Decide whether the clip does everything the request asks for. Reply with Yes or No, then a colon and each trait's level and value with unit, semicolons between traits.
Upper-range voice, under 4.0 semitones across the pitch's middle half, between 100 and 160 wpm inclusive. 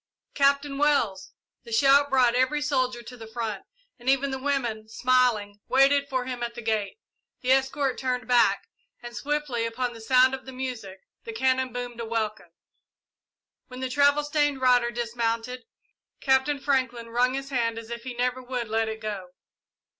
No: very high, 250 Hz; narrow, 2.5 semitones; average, 170 wpm